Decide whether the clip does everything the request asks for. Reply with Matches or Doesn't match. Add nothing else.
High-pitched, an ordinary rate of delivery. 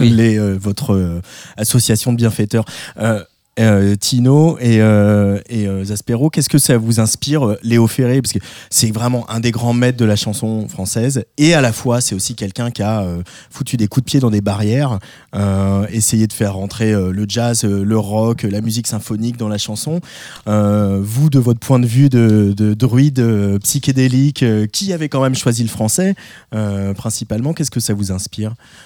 Doesn't match